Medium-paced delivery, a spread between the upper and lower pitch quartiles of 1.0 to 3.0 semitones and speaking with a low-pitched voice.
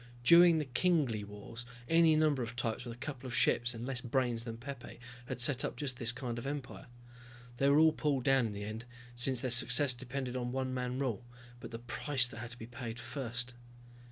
No: fast, 215 wpm; narrow, 2.4 semitones; low, 125 Hz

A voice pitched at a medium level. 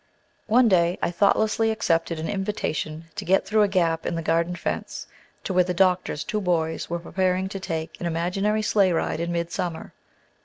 Yes: medium, 180 Hz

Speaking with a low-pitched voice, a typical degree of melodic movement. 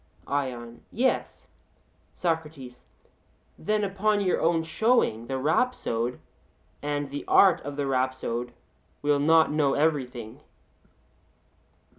No: medium, 145 Hz; average, 4.3 semitones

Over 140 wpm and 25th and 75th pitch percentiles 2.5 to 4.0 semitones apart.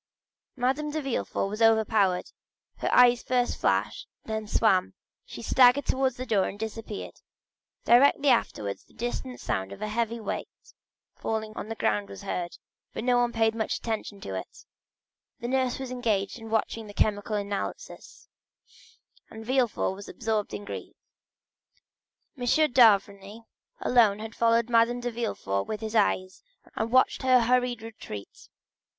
Yes: average, 155 wpm; average, 3.0 semitones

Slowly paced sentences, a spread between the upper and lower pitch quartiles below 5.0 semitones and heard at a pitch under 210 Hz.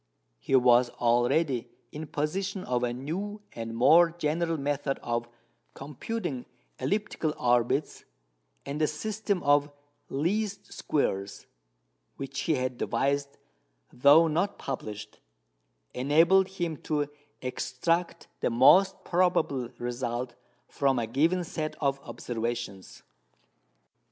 No: slow, 105 wpm; wide, 5.4 semitones; medium, 140 Hz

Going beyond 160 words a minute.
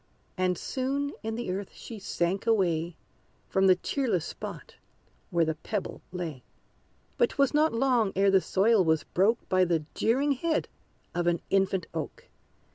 No: average, 155 wpm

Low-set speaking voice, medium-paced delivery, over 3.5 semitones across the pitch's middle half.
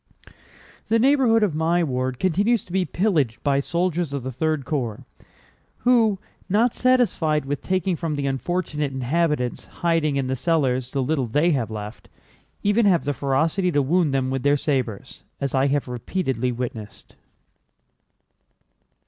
No: medium, 150 Hz; average, 150 wpm; wide, 5.4 semitones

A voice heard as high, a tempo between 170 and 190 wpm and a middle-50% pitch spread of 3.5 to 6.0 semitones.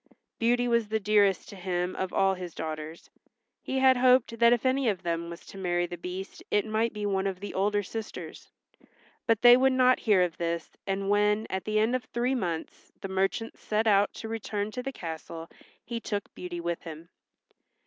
No: high, 205 Hz; average, 200 wpm; average, 4.3 semitones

